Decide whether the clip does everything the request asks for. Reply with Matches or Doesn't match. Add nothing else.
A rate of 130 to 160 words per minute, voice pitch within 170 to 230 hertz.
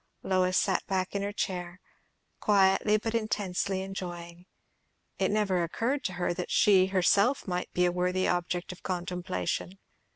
Matches